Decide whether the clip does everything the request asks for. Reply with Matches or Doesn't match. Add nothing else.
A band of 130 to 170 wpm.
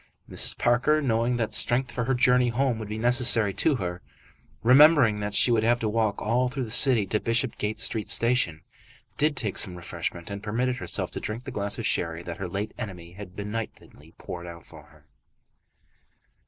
Doesn't match